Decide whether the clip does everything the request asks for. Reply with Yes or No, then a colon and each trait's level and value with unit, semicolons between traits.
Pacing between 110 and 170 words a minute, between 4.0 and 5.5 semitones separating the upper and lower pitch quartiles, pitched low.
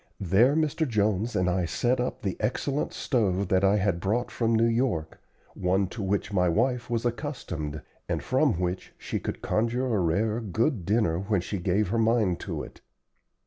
No: average, 185 wpm; average, 4.4 semitones; low, 105 Hz